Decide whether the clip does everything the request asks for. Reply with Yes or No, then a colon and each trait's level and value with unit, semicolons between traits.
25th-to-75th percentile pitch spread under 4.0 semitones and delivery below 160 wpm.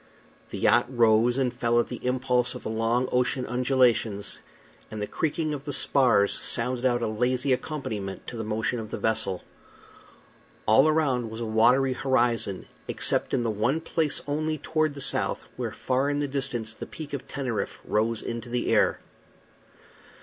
No: average, 3.3 semitones; average, 170 wpm